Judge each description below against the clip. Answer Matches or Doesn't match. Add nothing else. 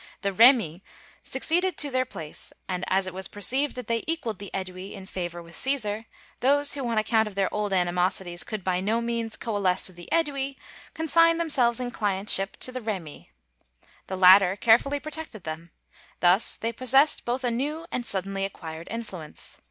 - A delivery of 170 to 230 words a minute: Matches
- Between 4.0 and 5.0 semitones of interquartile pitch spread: Doesn't match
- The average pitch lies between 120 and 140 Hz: Doesn't match